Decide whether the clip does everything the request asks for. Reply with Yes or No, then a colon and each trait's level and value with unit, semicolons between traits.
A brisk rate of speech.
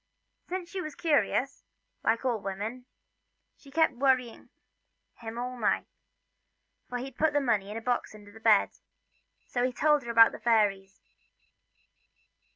No: average, 150 wpm